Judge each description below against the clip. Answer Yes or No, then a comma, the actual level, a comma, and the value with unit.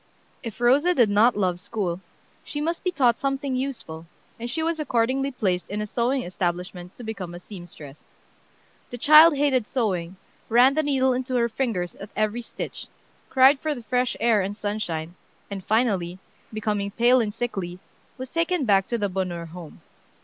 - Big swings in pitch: Yes, wide, 5.7 semitones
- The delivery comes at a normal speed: Yes, average, 170 wpm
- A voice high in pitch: Yes, high, 230 Hz